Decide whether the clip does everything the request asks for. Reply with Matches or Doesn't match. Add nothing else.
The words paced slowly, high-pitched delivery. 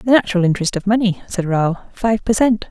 Doesn't match